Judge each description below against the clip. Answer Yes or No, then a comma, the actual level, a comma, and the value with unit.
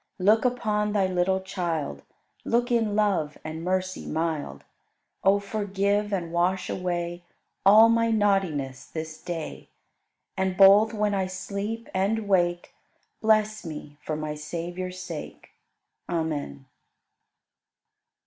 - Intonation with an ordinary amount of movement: Yes, average, 3.8 semitones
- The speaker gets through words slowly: Yes, slow, 115 wpm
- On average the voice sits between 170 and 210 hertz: Yes, medium, 185 Hz